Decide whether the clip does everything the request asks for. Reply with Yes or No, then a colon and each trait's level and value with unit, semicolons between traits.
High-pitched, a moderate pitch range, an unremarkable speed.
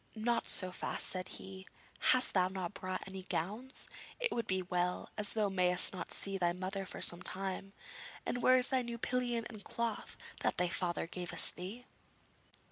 Yes: high, 195 Hz; average, 4.3 semitones; average, 180 wpm